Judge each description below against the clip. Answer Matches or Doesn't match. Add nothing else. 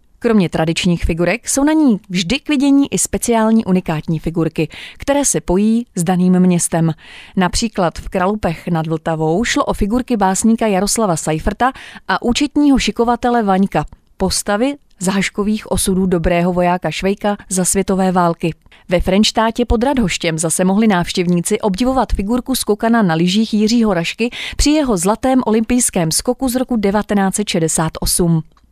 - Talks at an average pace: Matches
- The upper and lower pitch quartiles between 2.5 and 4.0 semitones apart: Doesn't match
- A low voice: Doesn't match